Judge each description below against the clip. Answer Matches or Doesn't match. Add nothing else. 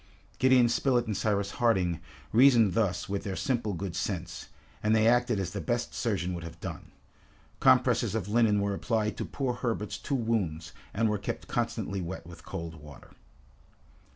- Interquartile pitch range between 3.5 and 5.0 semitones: Matches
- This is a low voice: Matches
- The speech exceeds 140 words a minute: Matches